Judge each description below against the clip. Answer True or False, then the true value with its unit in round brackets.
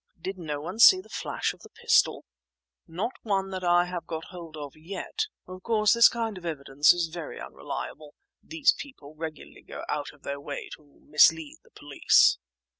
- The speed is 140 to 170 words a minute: False (185 wpm)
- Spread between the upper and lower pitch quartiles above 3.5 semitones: True (4.3 semitones)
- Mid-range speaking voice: True (170 Hz)